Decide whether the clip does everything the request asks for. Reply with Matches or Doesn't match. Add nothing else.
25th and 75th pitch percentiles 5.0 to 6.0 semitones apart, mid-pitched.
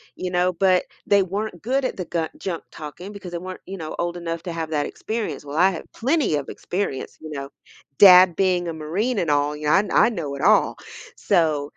Doesn't match